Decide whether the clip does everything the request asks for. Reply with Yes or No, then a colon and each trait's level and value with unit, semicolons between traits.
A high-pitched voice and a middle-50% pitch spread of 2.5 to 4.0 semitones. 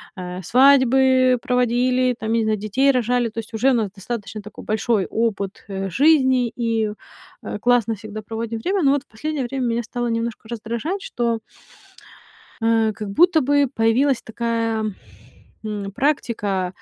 Yes: high, 230 Hz; average, 2.9 semitones